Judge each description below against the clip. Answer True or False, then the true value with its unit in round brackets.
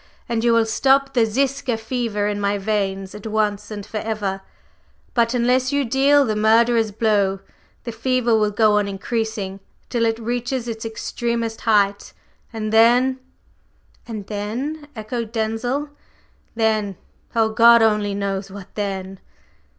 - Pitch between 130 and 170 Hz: False (225 Hz)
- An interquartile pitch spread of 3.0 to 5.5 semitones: False (2.4 semitones)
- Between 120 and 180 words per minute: True (145 wpm)